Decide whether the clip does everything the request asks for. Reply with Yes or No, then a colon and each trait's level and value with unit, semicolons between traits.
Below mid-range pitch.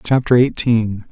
Yes: low, 115 Hz